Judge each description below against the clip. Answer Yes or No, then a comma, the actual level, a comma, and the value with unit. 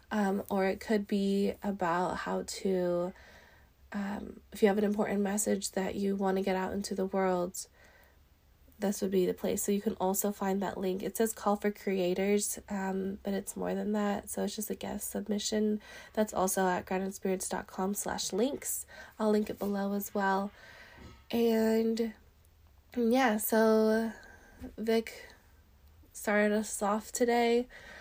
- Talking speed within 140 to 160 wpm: Yes, average, 155 wpm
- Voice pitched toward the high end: Yes, high, 200 Hz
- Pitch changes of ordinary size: No, narrow, 2.1 semitones